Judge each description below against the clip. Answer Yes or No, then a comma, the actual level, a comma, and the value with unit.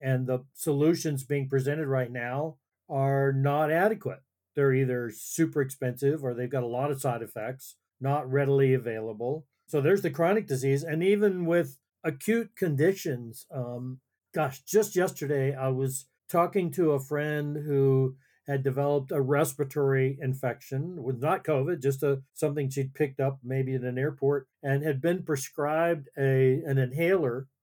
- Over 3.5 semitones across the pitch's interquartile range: No, average, 2.7 semitones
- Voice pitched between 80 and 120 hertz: No, medium, 140 Hz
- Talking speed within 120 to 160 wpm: Yes, average, 155 wpm